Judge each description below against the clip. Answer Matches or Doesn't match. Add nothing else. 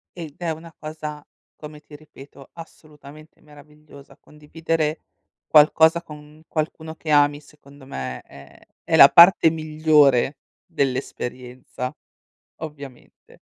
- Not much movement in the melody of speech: Matches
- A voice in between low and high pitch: Matches